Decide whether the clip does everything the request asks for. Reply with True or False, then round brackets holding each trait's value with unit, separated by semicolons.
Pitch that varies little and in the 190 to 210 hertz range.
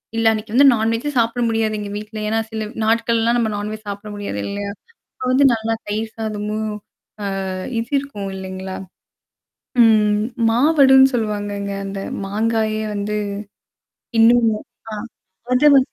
False (1.9 semitones; 220 Hz)